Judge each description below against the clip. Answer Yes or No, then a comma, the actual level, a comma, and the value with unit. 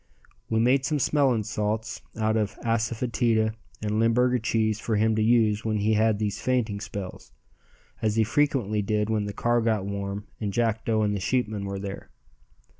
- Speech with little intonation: Yes, narrow, 1.8 semitones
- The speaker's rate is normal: Yes, average, 175 wpm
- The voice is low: Yes, low, 110 Hz